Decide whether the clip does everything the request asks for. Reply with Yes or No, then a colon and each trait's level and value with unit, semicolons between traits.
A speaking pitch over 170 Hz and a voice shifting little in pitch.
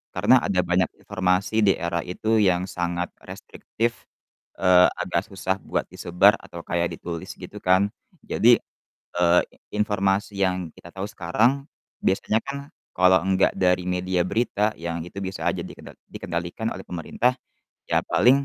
No: very low, 90 Hz; narrow, 2.2 semitones